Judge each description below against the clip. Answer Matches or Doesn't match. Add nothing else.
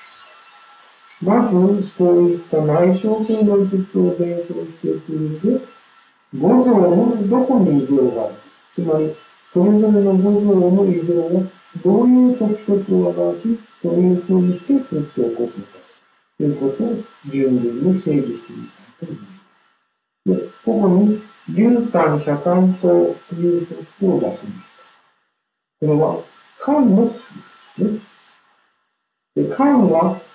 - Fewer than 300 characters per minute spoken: Matches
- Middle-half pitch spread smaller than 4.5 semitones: Doesn't match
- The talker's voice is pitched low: Doesn't match